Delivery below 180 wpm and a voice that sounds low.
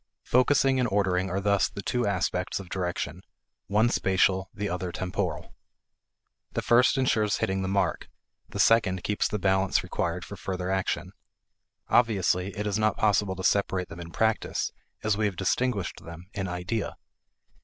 Yes: average, 160 wpm; very low, 95 Hz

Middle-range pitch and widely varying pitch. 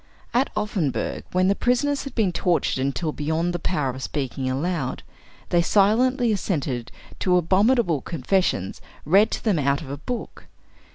Yes: medium, 175 Hz; wide, 6.8 semitones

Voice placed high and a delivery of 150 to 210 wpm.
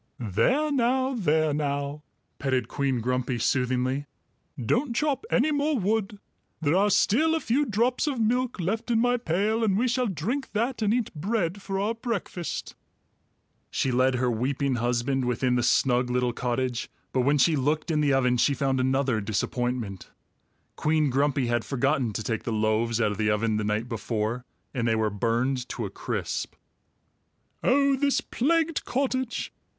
No: medium, 140 Hz; average, 165 wpm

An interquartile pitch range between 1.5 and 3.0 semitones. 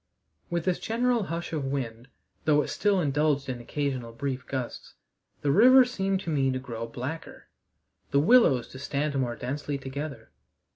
No: average, 4.7 semitones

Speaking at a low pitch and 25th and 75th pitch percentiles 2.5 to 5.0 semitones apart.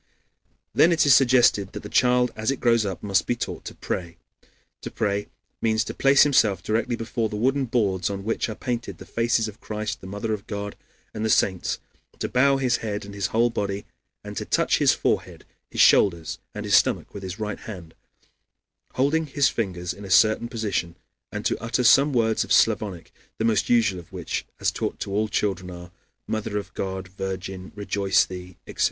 Yes: low, 105 Hz; average, 3.4 semitones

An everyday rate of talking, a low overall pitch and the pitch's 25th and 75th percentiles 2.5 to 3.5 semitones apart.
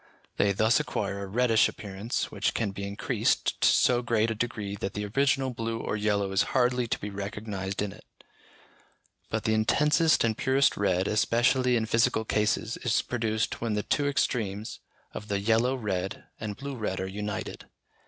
Yes: average, 175 wpm; low, 110 Hz; average, 3.1 semitones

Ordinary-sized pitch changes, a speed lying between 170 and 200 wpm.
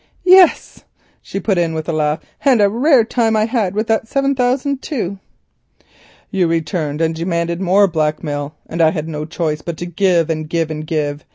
No: wide, 5.9 semitones; average, 190 wpm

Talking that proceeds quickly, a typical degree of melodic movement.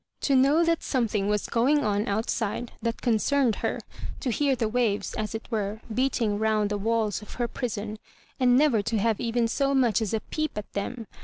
Yes: fast, 210 wpm; average, 3.2 semitones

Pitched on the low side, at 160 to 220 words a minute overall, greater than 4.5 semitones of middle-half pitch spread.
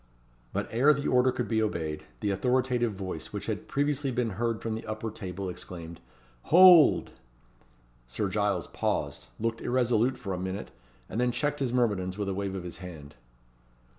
Yes: low, 110 Hz; average, 170 wpm; average, 4.9 semitones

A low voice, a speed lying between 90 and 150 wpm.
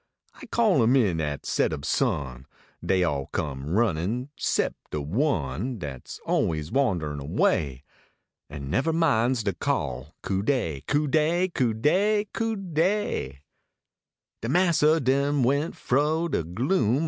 Yes: low, 120 Hz; average, 145 wpm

